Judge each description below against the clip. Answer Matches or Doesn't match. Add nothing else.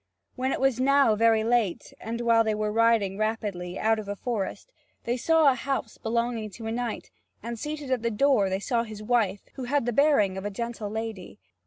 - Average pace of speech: Doesn't match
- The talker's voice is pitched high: Matches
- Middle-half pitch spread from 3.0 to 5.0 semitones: Doesn't match